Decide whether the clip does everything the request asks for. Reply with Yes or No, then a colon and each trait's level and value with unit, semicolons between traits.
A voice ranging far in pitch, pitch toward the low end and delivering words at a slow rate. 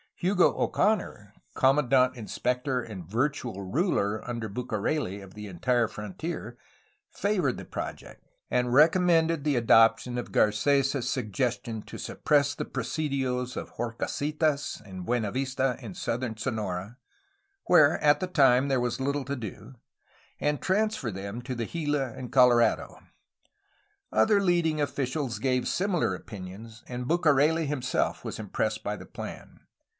No: average, 4.7 semitones; low, 125 Hz; slow, 130 wpm